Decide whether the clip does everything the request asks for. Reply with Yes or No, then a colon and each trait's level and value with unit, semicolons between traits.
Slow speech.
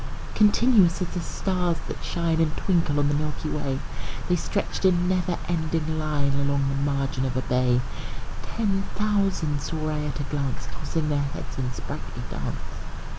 No: average, 170 wpm